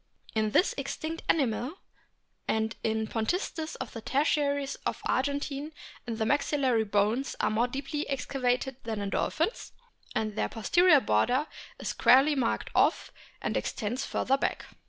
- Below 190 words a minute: Yes, average, 140 wpm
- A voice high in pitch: Yes, very high, 260 Hz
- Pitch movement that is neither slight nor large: Yes, average, 4.5 semitones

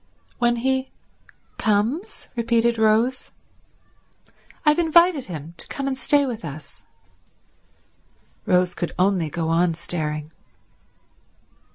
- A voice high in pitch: Yes, high, 220 Hz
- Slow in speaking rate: Yes, slow, 100 wpm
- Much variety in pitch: Yes, wide, 7.5 semitones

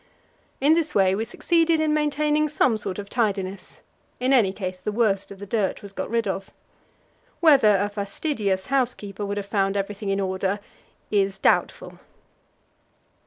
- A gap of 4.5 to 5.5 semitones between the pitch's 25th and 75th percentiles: Yes, average, 4.9 semitones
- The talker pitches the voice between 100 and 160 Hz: No, high, 205 Hz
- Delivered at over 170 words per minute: No, average, 160 wpm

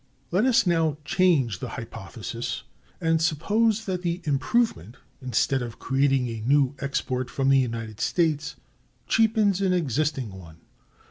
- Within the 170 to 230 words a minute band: No, slow, 135 wpm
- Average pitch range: No, wide, 6.2 semitones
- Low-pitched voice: No, medium, 145 Hz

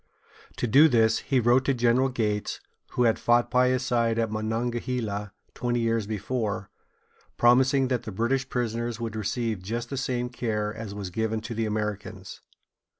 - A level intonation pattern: Yes, narrow, 2.3 semitones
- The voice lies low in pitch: Yes, low, 115 Hz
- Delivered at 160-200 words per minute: Yes, average, 165 wpm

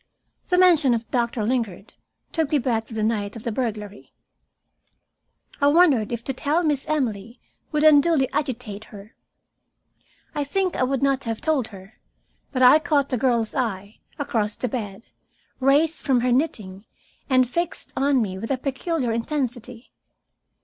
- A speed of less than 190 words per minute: Yes, average, 155 wpm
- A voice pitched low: No, very high, 250 Hz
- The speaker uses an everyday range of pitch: Yes, average, 4.4 semitones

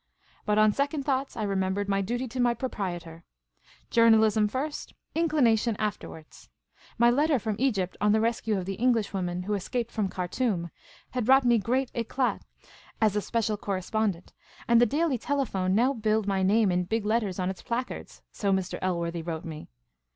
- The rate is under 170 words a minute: No, average, 175 wpm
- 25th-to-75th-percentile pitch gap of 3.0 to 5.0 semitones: Yes, average, 4.1 semitones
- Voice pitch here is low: No, high, 215 Hz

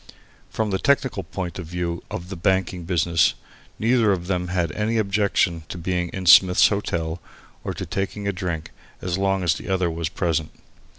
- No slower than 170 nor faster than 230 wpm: Yes, average, 180 wpm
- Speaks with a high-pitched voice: No, very low, 90 Hz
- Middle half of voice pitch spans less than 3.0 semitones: Yes, narrow, 2.4 semitones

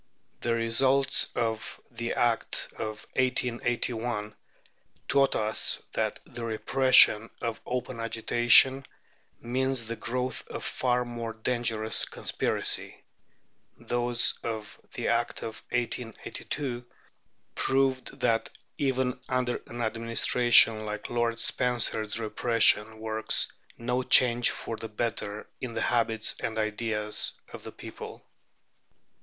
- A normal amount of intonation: No, narrow, 1.9 semitones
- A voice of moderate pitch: No, low, 115 Hz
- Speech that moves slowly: Yes, slow, 110 wpm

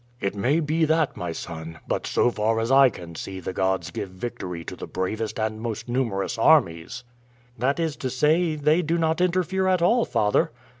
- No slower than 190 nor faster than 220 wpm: Yes, average, 195 wpm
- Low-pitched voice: Yes, low, 120 Hz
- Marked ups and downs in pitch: Yes, wide, 8.6 semitones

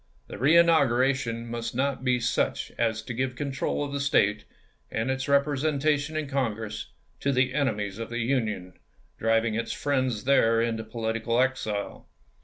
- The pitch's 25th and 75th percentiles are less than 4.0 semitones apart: Yes, average, 3.5 semitones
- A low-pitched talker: Yes, low, 125 Hz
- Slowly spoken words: No, average, 150 wpm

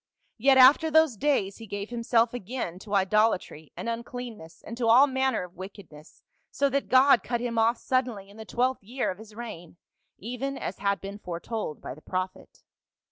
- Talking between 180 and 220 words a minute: Yes, average, 190 wpm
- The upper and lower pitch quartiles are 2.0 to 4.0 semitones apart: No, average, 4.5 semitones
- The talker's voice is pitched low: No, high, 230 Hz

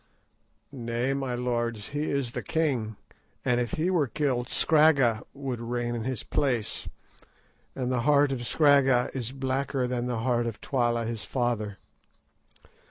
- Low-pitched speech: Yes, low, 125 Hz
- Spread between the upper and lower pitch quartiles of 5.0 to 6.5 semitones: No, narrow, 2.6 semitones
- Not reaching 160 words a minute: Yes, average, 150 wpm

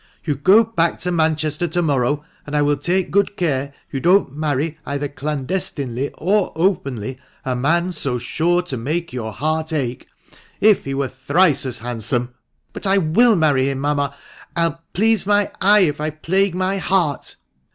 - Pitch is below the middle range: No, medium, 155 Hz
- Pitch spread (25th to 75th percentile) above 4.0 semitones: Yes, average, 4.7 semitones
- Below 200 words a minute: Yes, average, 185 wpm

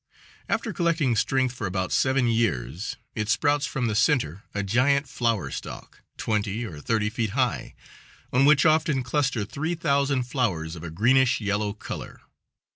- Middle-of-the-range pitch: No, low, 120 Hz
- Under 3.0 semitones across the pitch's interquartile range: No, average, 5.3 semitones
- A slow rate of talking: No, average, 155 wpm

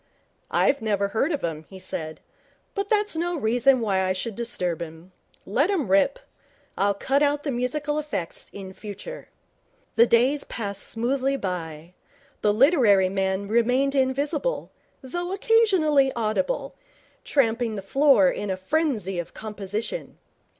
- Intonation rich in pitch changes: Yes, wide, 6.9 semitones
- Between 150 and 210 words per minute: No, average, 140 wpm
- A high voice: Yes, high, 235 Hz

